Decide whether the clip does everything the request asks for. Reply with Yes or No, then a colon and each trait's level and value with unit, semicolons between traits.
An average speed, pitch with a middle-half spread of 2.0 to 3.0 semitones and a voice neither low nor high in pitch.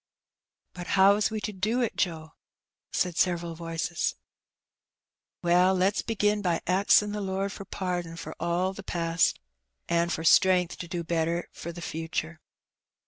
Yes: average, 150 wpm; narrow, 2.5 semitones; medium, 175 Hz